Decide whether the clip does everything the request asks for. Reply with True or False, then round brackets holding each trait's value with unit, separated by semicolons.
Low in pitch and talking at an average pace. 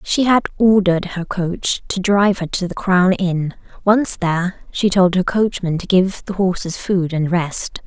False (185 Hz; 190 wpm)